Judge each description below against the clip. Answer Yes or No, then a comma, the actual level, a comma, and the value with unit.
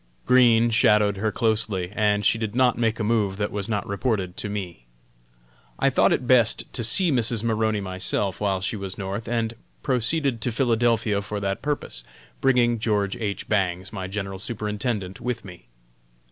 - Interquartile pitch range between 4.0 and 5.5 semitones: No, average, 3.0 semitones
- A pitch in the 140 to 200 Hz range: No, low, 105 Hz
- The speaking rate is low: No, average, 170 wpm